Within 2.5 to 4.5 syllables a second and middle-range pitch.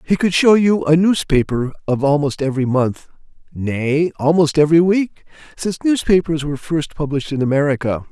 No: 5.4 syllables/s; medium, 155 Hz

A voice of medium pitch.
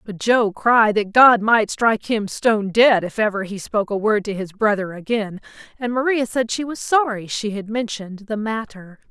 No: high, 215 Hz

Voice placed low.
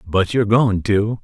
Yes: low, 105 Hz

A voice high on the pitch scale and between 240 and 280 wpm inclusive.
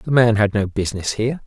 No: low, 110 Hz; fast, 245 wpm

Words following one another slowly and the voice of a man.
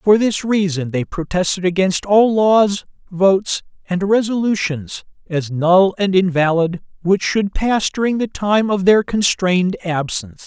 No: average, 145 wpm; male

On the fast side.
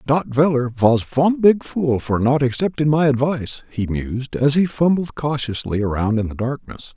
No: average, 180 wpm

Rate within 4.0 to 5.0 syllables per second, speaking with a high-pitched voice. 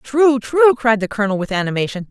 No: 5.8 syllables/s; high, 225 Hz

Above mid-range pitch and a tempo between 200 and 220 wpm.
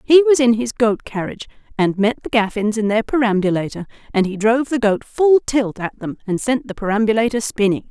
Yes: high, 225 Hz; fast, 205 wpm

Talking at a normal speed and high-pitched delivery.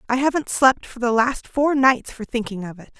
No: fast, 240 wpm; high, 245 Hz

